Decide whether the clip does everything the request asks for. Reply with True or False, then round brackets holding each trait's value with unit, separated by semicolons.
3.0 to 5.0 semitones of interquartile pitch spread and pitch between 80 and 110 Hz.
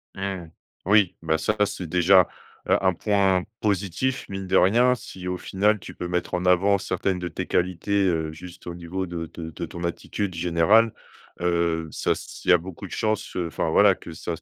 False (2.5 semitones; 90 Hz)